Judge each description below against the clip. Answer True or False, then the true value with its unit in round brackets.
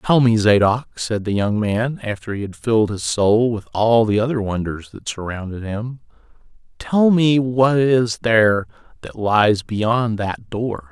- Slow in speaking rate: False (165 wpm)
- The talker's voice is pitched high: False (115 Hz)